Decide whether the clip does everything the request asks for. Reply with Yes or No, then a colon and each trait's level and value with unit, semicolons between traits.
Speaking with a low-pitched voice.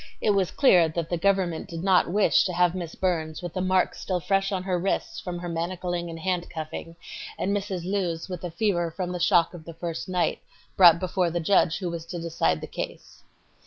No: medium, 175 Hz